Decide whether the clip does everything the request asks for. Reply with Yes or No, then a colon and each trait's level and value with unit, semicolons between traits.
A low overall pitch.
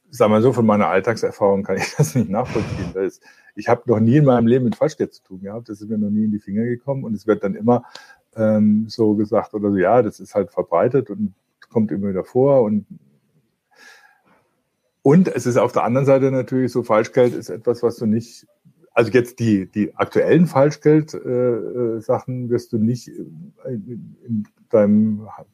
Yes: low, 115 Hz